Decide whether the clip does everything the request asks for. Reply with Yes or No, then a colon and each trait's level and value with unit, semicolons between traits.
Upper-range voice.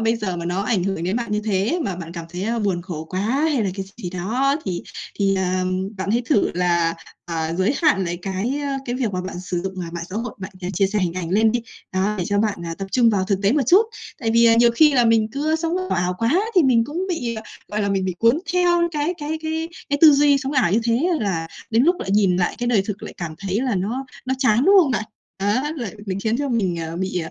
Yes: high, 210 Hz